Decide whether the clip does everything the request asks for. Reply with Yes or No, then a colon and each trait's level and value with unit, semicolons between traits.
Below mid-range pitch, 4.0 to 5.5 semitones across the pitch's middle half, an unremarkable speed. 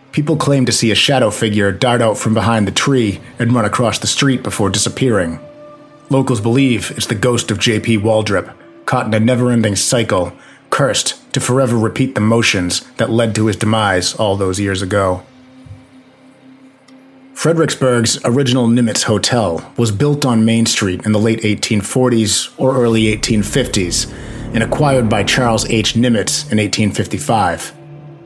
No: low, 115 Hz; average, 3.4 semitones; average, 155 wpm